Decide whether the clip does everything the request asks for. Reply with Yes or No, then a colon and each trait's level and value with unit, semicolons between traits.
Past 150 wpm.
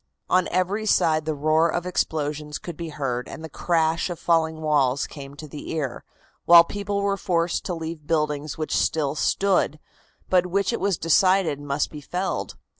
Yes: average, 180 wpm